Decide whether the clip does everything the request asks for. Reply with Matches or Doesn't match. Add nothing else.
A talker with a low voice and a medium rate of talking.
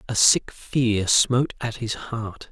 Matches